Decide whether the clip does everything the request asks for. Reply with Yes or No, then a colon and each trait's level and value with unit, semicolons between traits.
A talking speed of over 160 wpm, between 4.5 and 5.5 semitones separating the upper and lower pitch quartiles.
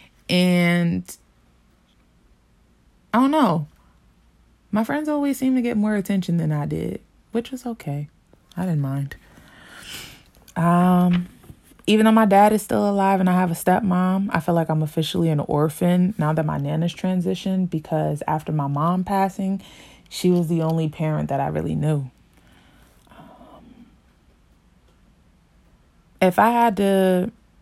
No: average, 140 wpm; average, 5.0 semitones